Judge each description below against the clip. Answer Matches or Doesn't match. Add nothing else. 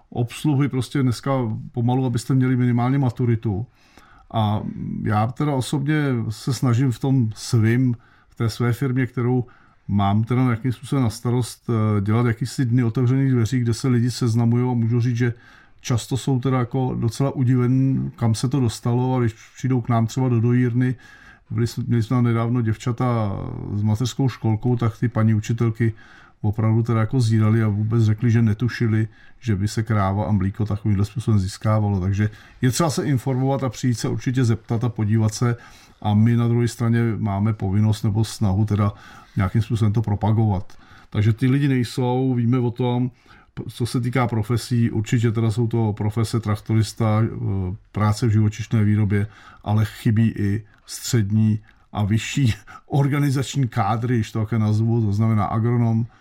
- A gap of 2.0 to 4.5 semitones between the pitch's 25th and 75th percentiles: Matches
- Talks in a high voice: Doesn't match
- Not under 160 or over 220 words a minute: Matches